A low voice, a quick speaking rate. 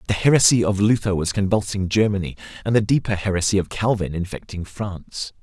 No: low, 100 Hz; average, 165 wpm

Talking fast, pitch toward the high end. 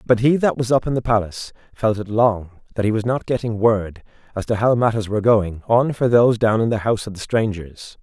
No: fast, 245 wpm; low, 110 Hz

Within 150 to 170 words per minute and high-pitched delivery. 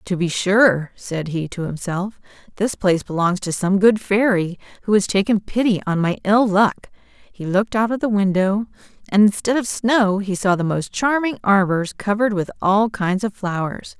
No: average, 190 wpm; high, 200 Hz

